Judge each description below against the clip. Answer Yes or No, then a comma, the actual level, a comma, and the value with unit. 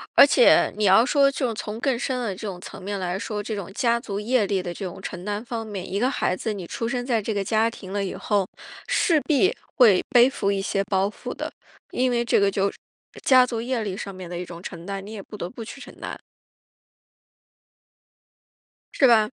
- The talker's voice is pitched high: Yes, high, 210 Hz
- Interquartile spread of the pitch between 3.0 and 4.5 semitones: Yes, average, 3.6 semitones